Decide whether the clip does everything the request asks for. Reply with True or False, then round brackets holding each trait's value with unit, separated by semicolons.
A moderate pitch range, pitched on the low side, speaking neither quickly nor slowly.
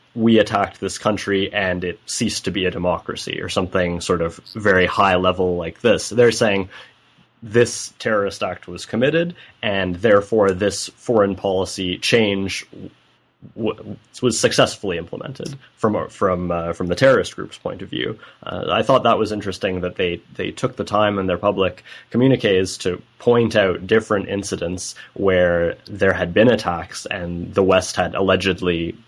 True (3.3 semitones; 95 Hz; 160 wpm)